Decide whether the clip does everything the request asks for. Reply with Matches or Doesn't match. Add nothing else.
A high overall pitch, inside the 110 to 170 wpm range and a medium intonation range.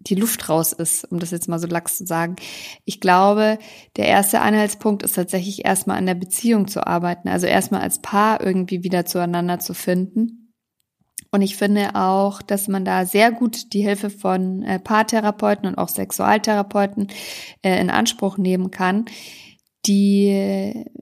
Doesn't match